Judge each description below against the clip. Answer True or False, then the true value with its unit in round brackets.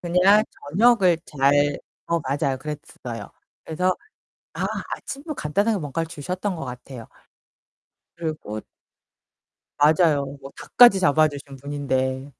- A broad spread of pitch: False (4.7 semitones)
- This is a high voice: False (150 Hz)